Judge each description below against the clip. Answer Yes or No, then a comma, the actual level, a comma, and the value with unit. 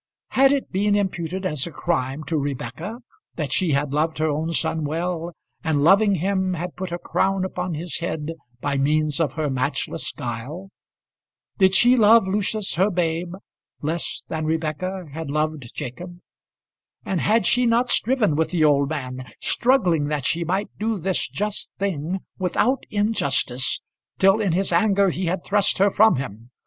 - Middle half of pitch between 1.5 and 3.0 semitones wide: No, average, 4.3 semitones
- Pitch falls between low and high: Yes, medium, 175 Hz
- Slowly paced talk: No, average, 165 wpm